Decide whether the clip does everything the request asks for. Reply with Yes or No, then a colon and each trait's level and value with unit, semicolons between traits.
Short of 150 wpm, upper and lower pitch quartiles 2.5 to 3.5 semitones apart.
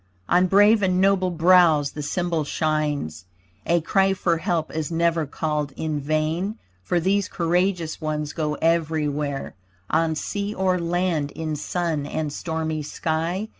Yes: average, 140 wpm; average, 2.9 semitones